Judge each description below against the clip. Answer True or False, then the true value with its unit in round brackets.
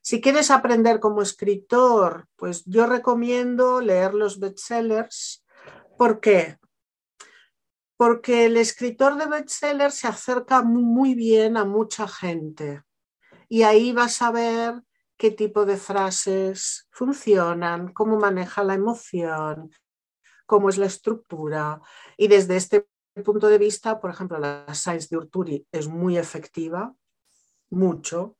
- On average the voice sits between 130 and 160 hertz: False (210 Hz)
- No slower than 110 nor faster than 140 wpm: True (125 wpm)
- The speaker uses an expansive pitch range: False (4.6 semitones)